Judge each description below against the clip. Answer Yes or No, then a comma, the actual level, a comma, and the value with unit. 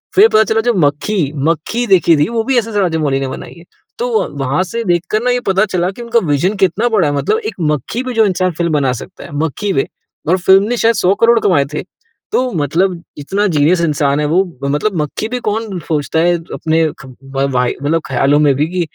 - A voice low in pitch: No, medium, 175 Hz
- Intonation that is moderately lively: No, wide, 6.4 semitones